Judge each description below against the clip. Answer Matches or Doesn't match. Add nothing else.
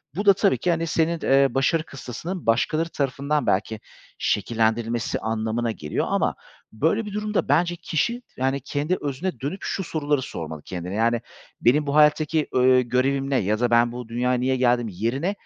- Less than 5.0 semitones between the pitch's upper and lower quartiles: Doesn't match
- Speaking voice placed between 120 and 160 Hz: Matches